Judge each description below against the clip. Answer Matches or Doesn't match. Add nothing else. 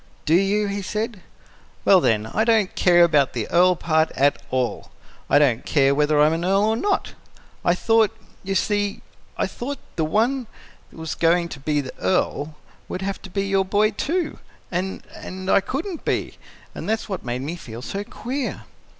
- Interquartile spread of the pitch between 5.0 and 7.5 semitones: Matches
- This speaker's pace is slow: Doesn't match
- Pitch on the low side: Doesn't match